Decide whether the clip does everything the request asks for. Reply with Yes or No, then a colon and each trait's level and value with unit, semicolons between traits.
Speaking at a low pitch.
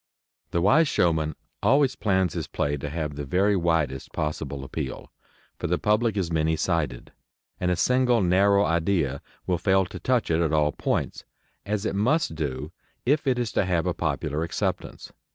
Yes: very low, 85 Hz